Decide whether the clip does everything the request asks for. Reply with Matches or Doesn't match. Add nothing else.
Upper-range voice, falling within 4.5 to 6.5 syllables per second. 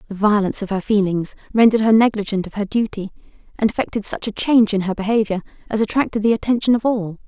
Doesn't match